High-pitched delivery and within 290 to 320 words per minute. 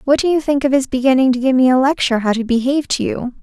Yes: very high, 260 Hz; fast, 300 wpm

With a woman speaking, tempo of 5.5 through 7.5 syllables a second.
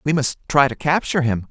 No: male; 6.1 syllables/s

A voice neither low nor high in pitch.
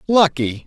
Yes: medium, 160 Hz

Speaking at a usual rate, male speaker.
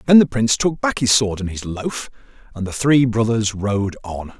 No: fast, 220 wpm; male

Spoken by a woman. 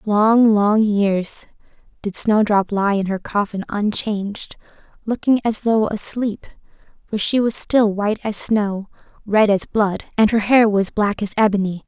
Yes: female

